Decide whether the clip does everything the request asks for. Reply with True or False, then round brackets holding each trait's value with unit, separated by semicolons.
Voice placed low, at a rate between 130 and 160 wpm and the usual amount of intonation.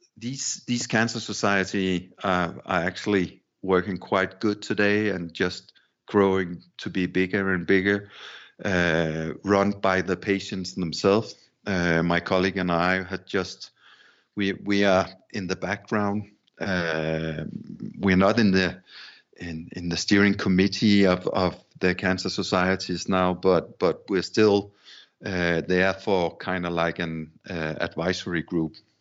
False (95 Hz; 140 wpm; 2.3 semitones)